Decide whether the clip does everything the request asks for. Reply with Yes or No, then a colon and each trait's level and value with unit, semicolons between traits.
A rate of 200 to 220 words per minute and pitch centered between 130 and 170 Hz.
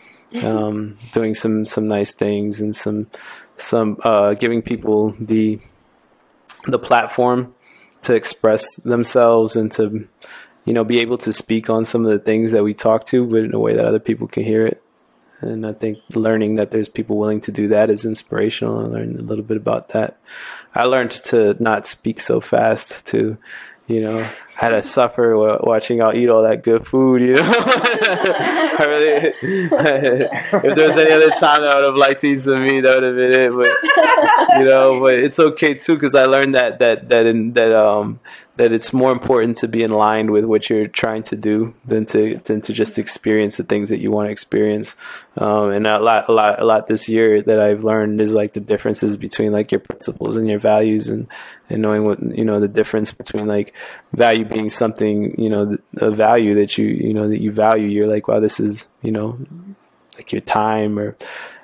No: fast, 205 wpm; low, 110 Hz